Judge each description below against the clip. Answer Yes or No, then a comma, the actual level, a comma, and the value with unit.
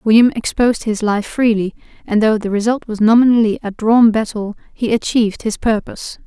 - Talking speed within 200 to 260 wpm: No, average, 170 wpm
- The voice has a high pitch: Yes, high, 220 Hz